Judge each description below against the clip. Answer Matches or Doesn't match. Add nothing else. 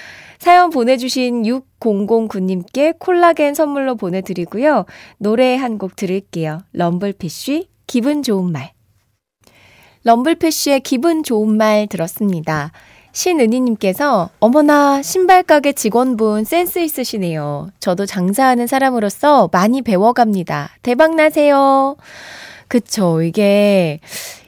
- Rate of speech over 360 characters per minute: Doesn't match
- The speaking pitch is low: Doesn't match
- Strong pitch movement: Matches